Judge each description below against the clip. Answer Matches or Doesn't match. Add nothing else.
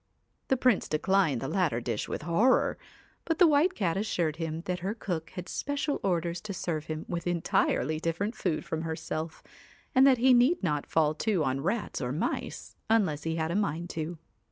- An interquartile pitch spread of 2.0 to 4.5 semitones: Doesn't match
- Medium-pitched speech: Matches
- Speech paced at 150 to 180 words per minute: Doesn't match